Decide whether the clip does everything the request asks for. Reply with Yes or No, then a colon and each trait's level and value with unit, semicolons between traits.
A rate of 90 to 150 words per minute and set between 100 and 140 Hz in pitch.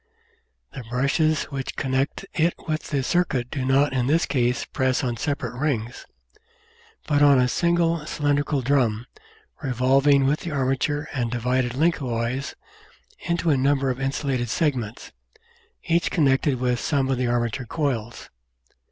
Yes: average, 145 wpm; low, 135 Hz